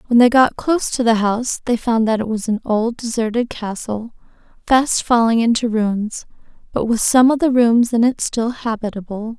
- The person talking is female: Yes, female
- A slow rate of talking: No, average, 190 wpm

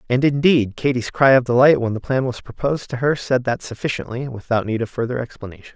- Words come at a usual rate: No, fast, 220 wpm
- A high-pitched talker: No, low, 125 Hz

